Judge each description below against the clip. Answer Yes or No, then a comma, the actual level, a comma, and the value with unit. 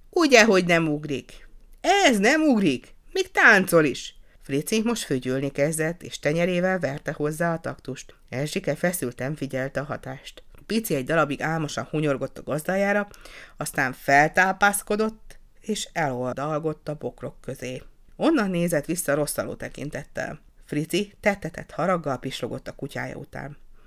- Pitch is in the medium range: Yes, medium, 155 Hz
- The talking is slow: No, average, 130 wpm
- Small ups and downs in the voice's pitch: No, wide, 5.5 semitones